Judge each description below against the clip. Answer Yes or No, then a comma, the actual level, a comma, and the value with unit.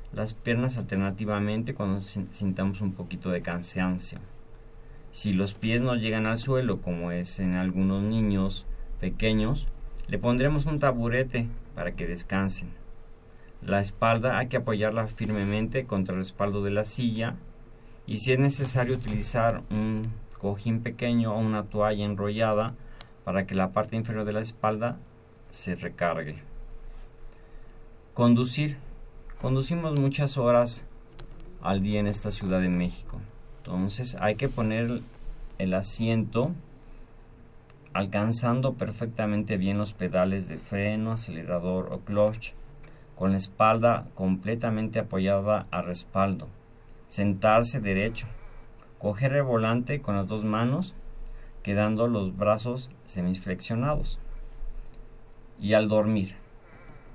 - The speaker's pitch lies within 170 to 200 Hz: No, low, 110 Hz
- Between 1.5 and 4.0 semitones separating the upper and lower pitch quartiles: Yes, average, 2.9 semitones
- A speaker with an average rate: No, slow, 120 wpm